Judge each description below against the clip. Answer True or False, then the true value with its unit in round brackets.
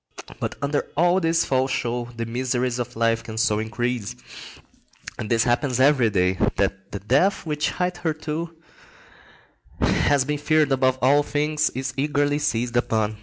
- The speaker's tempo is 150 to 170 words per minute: False (140 wpm)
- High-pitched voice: False (130 Hz)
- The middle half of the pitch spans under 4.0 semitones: False (4.3 semitones)